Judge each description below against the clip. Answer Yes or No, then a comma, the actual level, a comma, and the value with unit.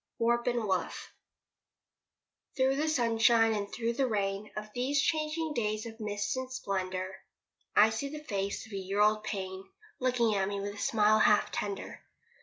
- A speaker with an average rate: Yes, average, 170 wpm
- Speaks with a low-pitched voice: No, high, 215 Hz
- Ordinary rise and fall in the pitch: Yes, average, 3.5 semitones